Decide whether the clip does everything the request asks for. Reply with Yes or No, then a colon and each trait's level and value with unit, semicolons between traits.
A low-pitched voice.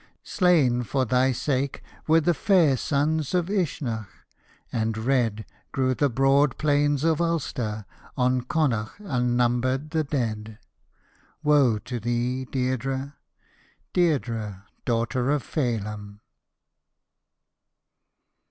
Yes: low, 130 Hz